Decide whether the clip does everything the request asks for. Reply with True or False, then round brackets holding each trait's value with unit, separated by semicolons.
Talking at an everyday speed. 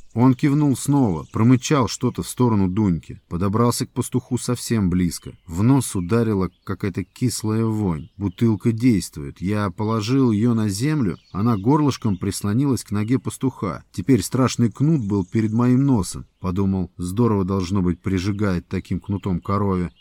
True (140 wpm)